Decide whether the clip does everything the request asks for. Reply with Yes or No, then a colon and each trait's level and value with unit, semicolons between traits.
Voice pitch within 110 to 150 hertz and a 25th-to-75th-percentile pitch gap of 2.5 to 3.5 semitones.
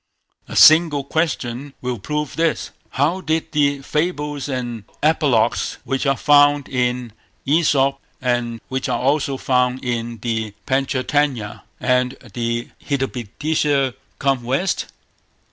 Yes: low, 135 Hz; average, 3.1 semitones